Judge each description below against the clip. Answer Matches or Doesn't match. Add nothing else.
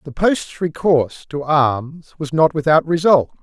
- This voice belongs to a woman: Doesn't match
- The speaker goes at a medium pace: Matches